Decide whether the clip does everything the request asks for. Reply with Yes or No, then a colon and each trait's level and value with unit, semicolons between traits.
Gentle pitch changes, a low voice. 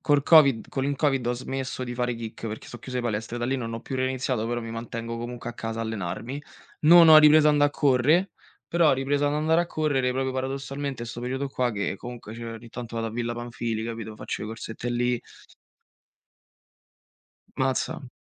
No: average, 3.0 semitones; low, 125 Hz